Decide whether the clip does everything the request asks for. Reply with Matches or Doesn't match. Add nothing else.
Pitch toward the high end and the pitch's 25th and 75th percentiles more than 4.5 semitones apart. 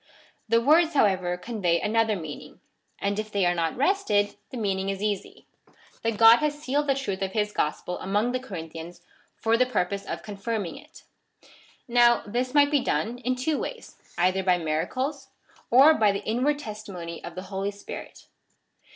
Matches